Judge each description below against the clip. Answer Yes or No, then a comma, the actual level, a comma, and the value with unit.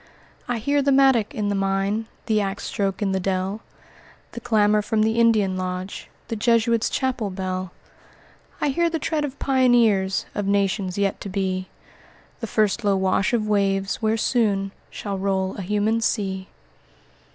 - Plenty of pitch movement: No, average, 2.9 semitones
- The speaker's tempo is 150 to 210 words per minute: Yes, average, 165 wpm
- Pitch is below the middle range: No, high, 205 Hz